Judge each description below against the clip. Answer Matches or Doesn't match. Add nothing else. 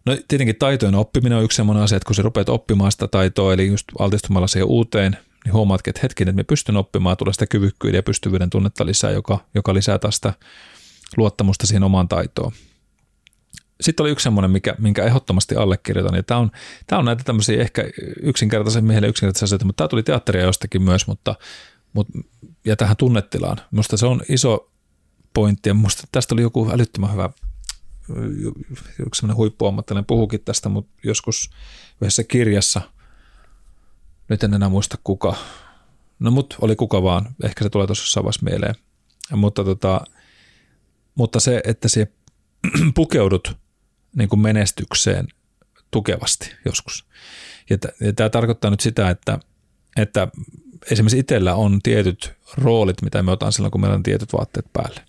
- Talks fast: Matches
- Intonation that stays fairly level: Doesn't match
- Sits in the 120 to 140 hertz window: Doesn't match